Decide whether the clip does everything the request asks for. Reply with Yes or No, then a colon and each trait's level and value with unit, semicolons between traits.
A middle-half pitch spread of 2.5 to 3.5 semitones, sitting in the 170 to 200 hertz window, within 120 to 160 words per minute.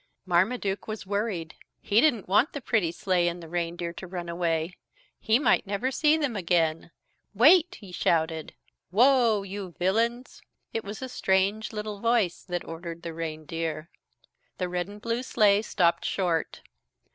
No: average, 4.6 semitones; high, 190 Hz; average, 155 wpm